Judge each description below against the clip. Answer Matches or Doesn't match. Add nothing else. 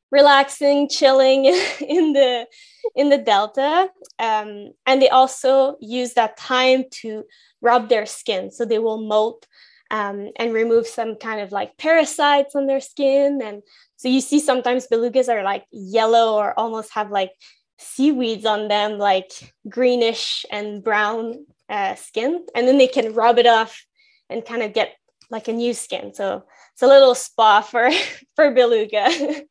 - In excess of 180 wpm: Doesn't match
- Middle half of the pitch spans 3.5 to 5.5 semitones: Matches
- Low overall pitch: Doesn't match